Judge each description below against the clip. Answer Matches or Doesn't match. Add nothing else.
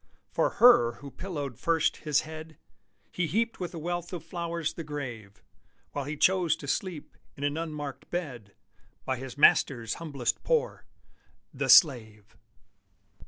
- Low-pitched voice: Doesn't match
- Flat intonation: Doesn't match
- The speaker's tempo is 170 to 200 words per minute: Doesn't match